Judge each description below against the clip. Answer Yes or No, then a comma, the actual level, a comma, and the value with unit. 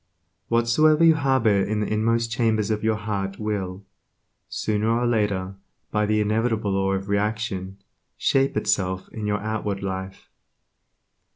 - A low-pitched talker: Yes, low, 105 Hz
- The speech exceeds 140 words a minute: No, slow, 135 wpm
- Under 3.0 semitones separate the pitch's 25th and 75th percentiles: Yes, narrow, 2.6 semitones